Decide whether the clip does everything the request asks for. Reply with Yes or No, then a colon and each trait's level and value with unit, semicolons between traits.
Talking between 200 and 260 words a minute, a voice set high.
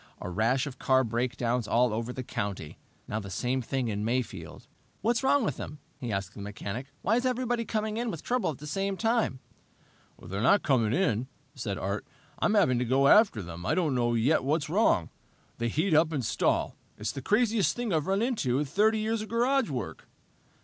No: fast, 205 wpm; low, 135 Hz